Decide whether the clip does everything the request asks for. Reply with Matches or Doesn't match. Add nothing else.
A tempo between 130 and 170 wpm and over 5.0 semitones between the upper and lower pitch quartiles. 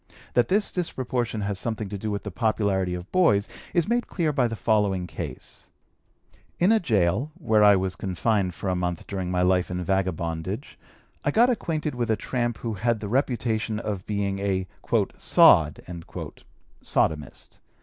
Doesn't match